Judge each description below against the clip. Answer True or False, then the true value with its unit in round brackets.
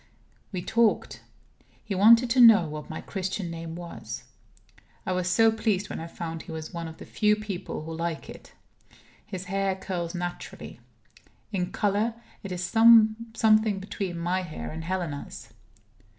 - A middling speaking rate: True (155 wpm)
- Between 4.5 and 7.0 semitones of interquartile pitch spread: False (4.0 semitones)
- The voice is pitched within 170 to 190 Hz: True (185 Hz)